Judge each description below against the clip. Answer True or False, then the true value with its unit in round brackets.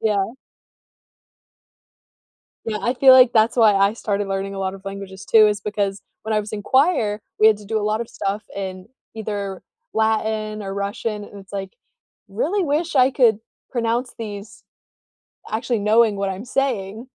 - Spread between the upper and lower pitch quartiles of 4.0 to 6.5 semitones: False (2.6 semitones)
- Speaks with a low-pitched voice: False (215 Hz)